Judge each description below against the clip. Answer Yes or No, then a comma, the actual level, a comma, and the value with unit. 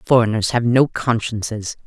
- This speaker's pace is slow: Yes, slow, 130 wpm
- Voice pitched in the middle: No, low, 115 Hz